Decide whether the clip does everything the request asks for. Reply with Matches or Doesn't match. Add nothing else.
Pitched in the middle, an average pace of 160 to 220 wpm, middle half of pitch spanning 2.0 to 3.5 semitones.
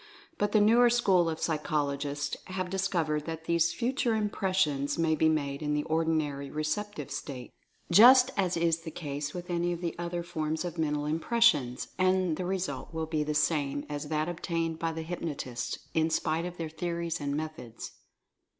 Matches